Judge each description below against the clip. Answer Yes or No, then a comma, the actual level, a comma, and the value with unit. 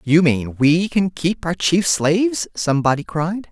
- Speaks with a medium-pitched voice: Yes, medium, 160 Hz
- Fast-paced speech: No, average, 170 wpm